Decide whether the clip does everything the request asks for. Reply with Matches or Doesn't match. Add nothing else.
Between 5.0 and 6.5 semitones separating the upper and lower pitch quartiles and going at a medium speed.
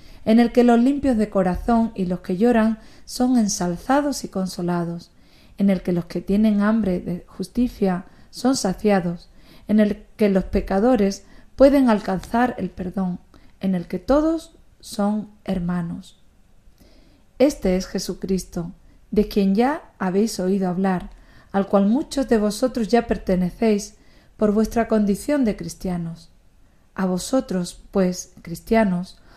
Doesn't match